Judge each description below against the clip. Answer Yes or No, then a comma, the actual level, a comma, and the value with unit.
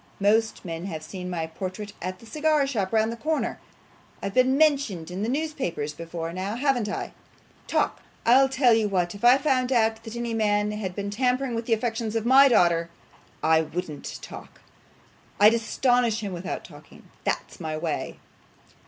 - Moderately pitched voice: No, high, 220 Hz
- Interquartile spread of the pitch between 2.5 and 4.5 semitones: No, average, 5.3 semitones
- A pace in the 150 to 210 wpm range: Yes, average, 175 wpm